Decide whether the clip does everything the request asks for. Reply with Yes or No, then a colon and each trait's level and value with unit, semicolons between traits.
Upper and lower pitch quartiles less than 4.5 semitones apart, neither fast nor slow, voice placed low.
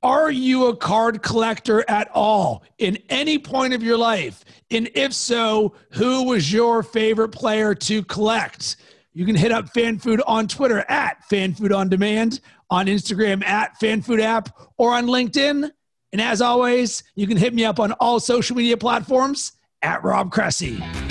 No: narrow, 2.4 semitones; average, 175 wpm; high, 225 Hz